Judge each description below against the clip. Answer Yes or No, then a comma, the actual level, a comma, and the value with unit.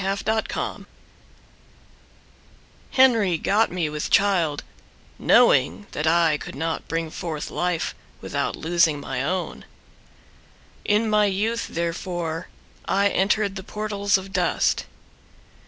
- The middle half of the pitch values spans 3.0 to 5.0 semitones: Yes, average, 3.9 semitones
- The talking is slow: Yes, slow, 110 wpm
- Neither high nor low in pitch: Yes, medium, 180 Hz